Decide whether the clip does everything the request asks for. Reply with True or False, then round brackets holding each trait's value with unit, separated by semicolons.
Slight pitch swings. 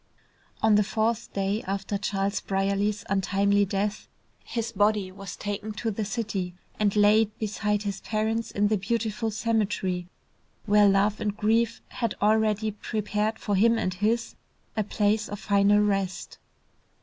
True (1.6 semitones)